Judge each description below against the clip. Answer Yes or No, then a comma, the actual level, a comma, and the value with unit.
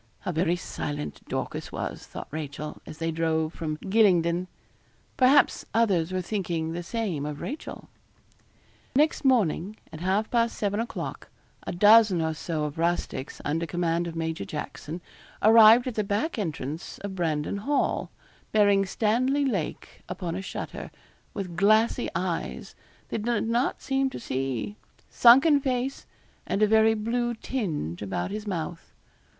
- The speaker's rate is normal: Yes, average, 145 wpm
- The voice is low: No, high, 190 Hz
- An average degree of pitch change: No, wide, 5.7 semitones